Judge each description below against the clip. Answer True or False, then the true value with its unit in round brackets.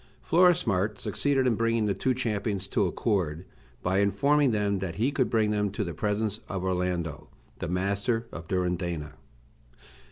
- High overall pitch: False (100 Hz)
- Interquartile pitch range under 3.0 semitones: False (4.0 semitones)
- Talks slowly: False (155 wpm)